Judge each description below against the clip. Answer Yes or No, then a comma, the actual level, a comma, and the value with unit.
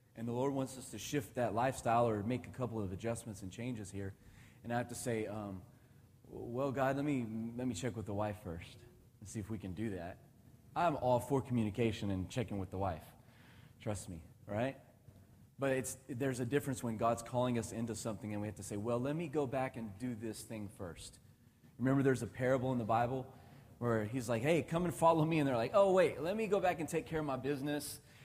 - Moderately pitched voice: No, low, 120 Hz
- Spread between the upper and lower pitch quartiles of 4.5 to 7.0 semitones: No, average, 3.2 semitones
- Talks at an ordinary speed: No, fast, 235 wpm